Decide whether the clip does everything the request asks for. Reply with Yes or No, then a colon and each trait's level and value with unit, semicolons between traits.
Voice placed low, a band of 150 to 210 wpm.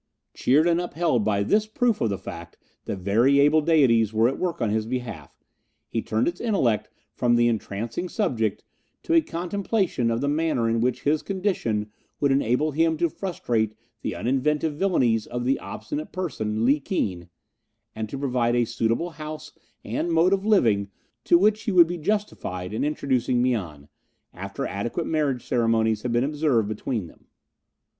Yes: low, 130 Hz; average, 170 wpm